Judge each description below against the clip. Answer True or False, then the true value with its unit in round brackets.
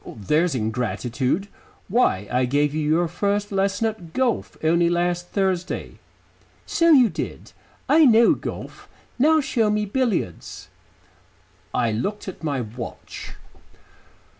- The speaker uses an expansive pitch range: True (7.0 semitones)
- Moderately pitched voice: True (175 Hz)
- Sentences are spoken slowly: True (120 wpm)